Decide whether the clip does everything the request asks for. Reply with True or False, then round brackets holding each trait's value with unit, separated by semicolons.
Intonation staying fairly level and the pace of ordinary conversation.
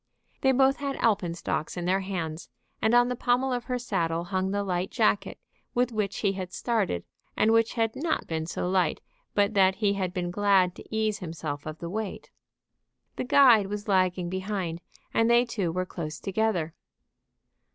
False (4.2 semitones; 180 wpm)